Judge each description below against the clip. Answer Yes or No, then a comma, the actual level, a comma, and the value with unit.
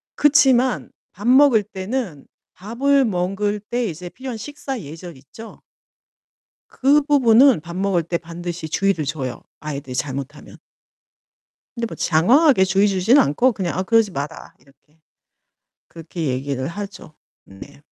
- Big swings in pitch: Yes, wide, 7.3 semitones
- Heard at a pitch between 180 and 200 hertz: Yes, high, 190 Hz